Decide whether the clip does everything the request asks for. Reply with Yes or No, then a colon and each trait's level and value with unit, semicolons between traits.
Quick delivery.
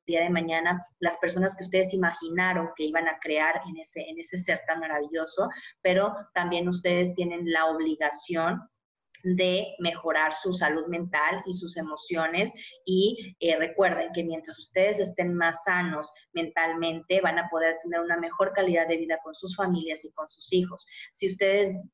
No: average, 165 wpm